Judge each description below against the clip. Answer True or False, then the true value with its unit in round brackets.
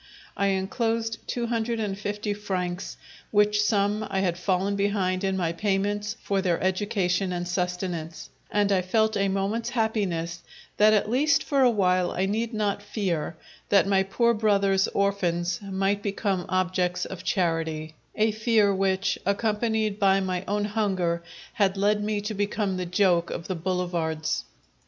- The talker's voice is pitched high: True (195 Hz)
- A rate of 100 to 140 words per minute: False (155 wpm)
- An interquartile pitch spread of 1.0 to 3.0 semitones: True (2.4 semitones)